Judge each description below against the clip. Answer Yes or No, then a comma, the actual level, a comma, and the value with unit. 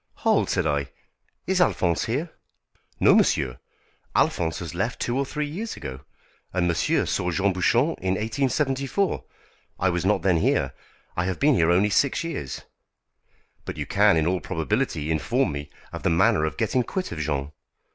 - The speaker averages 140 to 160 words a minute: No, average, 170 wpm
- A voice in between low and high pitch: No, very low, 95 Hz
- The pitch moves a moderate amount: No, wide, 8.6 semitones